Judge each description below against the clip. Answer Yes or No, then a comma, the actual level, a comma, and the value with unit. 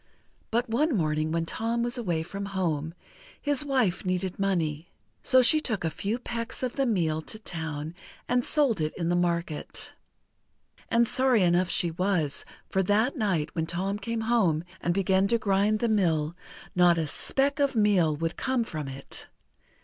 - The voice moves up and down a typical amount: No, wide, 5.9 semitones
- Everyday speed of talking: Yes, average, 170 wpm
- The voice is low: No, high, 190 Hz